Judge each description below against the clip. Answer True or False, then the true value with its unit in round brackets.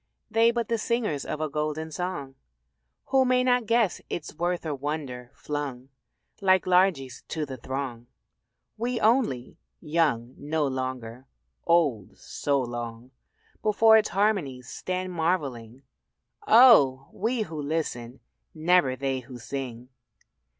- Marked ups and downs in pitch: True (6.4 semitones)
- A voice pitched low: False (150 Hz)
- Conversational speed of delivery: False (125 wpm)